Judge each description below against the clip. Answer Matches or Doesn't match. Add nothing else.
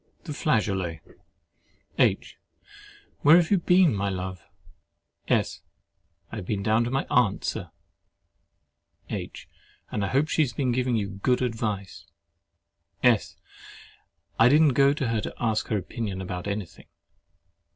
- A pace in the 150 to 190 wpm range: Doesn't match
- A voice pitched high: Doesn't match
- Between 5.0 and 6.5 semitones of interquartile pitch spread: Matches